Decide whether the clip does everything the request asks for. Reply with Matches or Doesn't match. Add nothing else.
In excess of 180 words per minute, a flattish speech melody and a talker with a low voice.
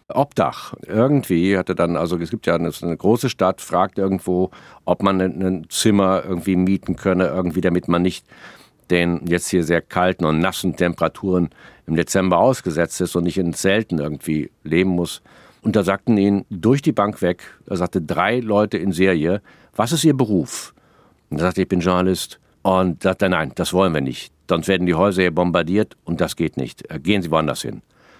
Matches